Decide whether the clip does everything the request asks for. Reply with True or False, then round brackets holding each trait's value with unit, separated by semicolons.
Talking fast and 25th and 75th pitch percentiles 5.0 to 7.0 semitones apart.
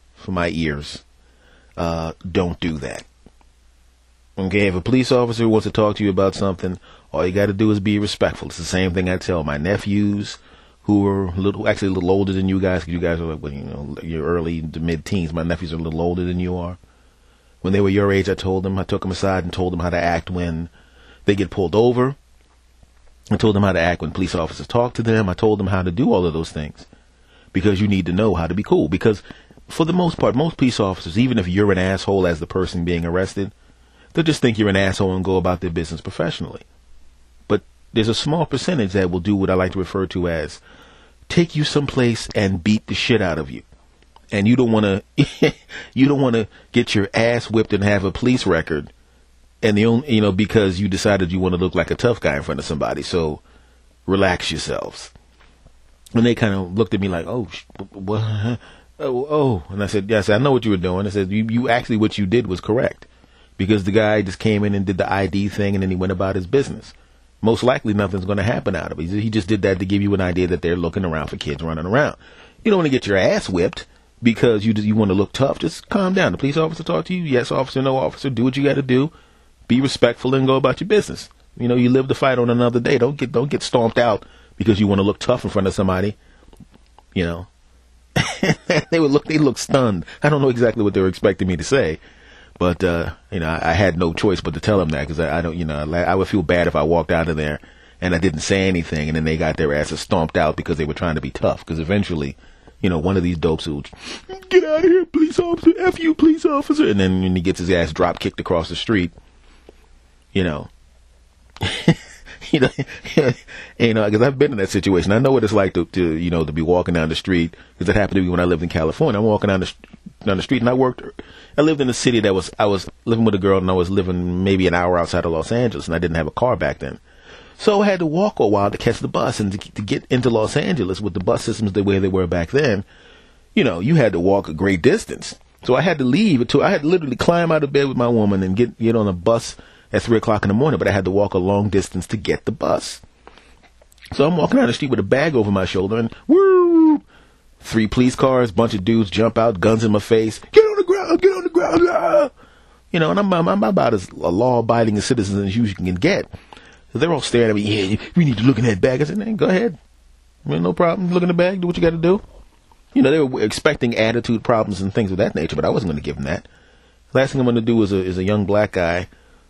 True (260 wpm; 5.4 semitones)